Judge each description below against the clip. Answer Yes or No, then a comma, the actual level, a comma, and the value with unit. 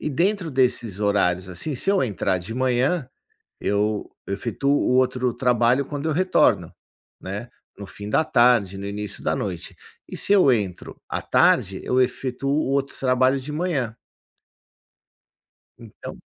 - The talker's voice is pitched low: Yes, low, 125 Hz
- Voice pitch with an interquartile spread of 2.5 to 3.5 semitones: No, average, 5.1 semitones